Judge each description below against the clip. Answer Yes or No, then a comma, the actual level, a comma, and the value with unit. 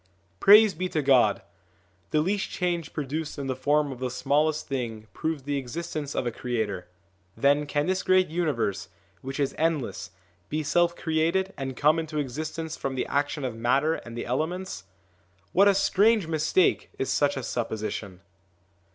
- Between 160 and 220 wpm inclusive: Yes, average, 165 wpm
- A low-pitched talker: No, medium, 150 Hz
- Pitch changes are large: No, average, 4.1 semitones